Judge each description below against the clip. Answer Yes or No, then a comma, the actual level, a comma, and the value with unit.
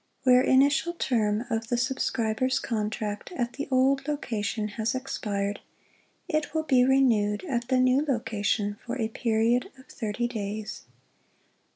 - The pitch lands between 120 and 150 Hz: No, high, 240 Hz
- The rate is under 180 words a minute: Yes, average, 140 wpm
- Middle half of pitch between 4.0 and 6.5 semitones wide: No, average, 3.6 semitones